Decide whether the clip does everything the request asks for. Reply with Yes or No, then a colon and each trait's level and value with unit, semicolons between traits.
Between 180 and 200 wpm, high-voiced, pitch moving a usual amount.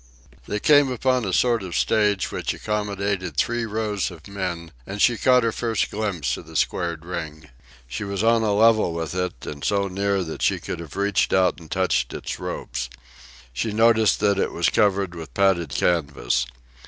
No: average, 185 wpm; low, 100 Hz; average, 4.3 semitones